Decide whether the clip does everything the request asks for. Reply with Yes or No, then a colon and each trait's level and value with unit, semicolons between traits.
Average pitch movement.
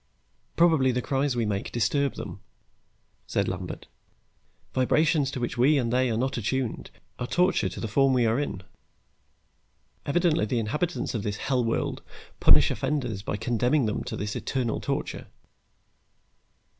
Yes: average, 3.7 semitones